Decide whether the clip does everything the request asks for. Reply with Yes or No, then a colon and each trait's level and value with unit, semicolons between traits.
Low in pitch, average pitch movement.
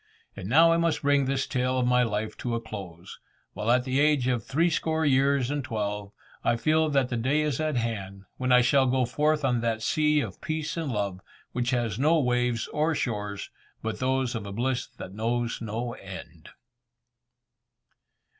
Yes: low, 125 Hz; average, 3.9 semitones